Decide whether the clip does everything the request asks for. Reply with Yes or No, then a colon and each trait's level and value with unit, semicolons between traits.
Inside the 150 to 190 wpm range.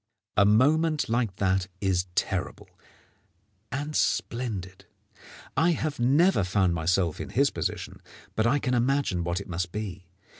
No: average, 140 wpm